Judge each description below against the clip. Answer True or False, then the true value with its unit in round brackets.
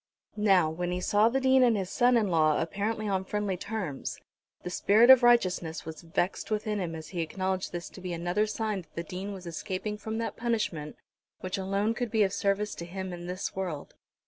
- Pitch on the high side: True (195 Hz)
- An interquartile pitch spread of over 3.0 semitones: True (3.5 semitones)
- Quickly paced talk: True (210 wpm)